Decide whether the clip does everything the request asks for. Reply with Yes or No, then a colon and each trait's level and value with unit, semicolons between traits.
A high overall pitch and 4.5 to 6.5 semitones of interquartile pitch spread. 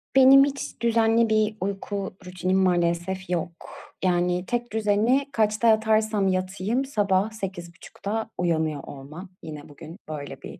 No: high, 195 Hz; average, 3.9 semitones